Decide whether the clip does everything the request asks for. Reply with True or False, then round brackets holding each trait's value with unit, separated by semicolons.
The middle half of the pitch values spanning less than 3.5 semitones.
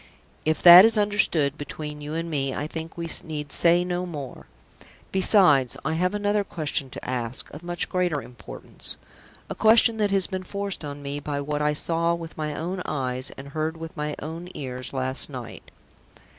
False (3.9 semitones)